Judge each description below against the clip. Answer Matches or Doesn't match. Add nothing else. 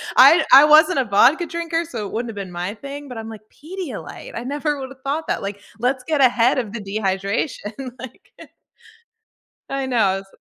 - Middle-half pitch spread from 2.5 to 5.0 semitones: Doesn't match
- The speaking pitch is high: Matches